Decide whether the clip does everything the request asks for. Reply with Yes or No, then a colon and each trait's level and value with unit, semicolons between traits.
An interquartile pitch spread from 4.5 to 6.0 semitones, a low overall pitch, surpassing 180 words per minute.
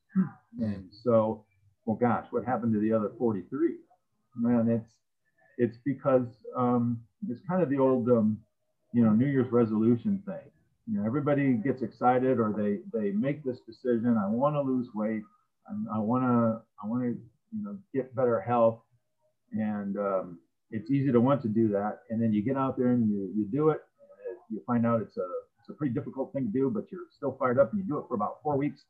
Yes: average, 4.8 semitones; low, 120 Hz; fast, 205 wpm